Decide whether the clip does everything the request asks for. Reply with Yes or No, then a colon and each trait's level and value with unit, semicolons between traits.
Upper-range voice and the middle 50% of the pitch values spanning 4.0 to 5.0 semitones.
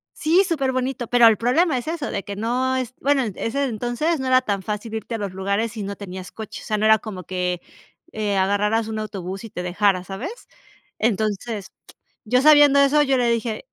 Yes: high, 225 Hz; average, 4.4 semitones